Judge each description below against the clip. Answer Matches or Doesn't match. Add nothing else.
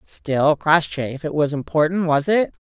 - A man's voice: Doesn't match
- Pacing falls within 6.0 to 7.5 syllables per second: Doesn't match